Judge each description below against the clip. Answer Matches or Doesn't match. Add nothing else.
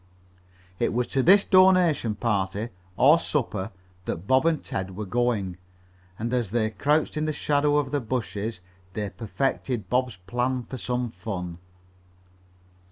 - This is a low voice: Matches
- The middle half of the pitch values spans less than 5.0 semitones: Doesn't match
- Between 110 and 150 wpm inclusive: Matches